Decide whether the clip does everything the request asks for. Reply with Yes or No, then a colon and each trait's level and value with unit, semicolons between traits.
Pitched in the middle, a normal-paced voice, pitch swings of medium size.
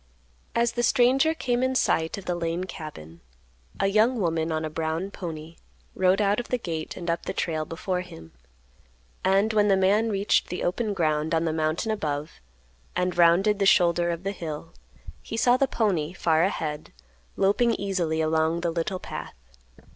Yes: medium, 180 Hz; average, 175 wpm; average, 4.2 semitones